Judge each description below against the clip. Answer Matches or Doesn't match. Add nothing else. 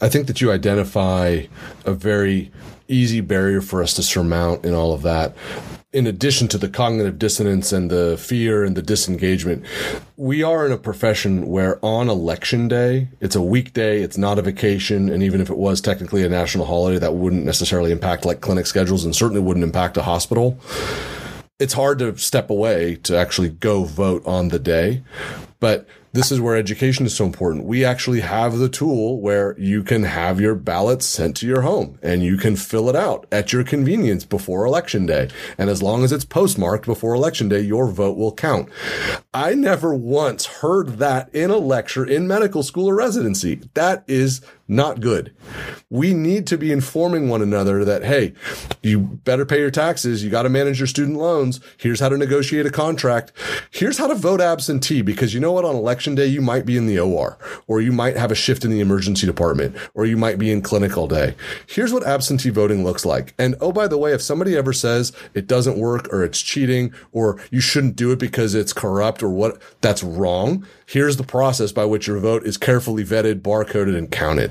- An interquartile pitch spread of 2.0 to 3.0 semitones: Doesn't match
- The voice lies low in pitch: Matches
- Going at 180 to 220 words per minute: Matches